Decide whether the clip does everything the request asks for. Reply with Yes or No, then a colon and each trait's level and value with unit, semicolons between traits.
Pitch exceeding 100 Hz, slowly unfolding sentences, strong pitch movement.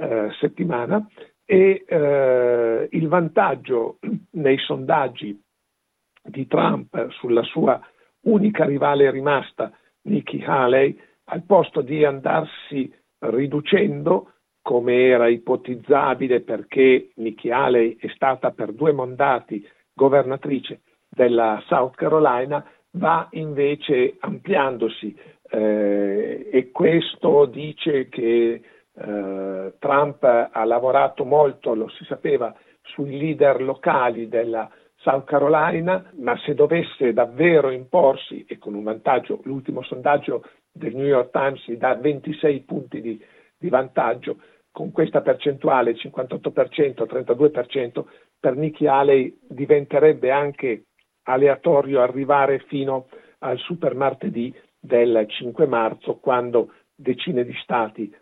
No: low, 135 Hz; slow, 105 wpm; average, 3.8 semitones